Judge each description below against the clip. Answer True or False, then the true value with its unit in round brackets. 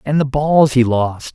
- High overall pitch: False (135 Hz)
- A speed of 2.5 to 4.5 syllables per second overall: True (4.0 syllables/s)